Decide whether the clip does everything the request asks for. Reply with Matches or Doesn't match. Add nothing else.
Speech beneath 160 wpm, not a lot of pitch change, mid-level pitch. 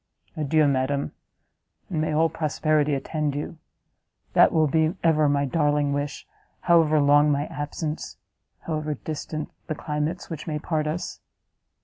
Matches